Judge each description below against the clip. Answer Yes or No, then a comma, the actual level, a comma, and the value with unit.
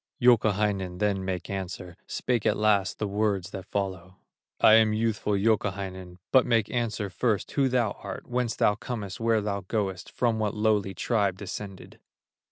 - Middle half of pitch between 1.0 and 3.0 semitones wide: Yes, average, 2.7 semitones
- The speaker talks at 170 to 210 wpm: No, average, 160 wpm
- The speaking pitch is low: Yes, low, 105 Hz